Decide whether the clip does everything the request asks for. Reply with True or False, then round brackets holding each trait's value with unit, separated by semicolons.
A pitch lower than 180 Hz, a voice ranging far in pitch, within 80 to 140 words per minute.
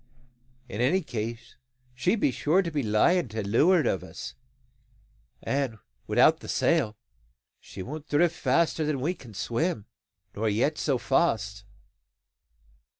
True (135 Hz; 6.6 semitones; 135 wpm)